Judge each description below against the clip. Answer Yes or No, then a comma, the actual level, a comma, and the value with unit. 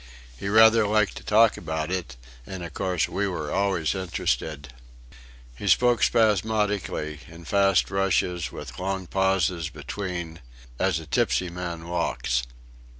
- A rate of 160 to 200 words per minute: No, slow, 135 wpm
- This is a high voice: No, very low, 90 Hz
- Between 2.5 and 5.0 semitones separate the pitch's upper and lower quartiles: Yes, average, 3.3 semitones